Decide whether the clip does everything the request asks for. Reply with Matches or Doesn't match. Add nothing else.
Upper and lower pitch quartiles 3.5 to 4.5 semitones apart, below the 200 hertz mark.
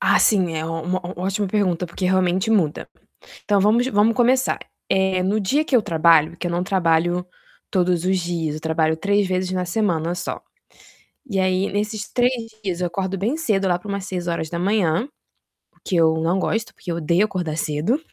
Doesn't match